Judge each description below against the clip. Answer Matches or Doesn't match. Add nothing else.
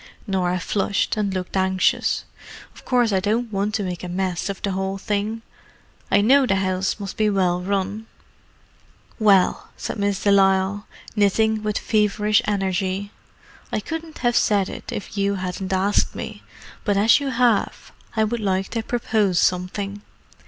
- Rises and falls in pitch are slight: Matches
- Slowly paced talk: Doesn't match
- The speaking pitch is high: Matches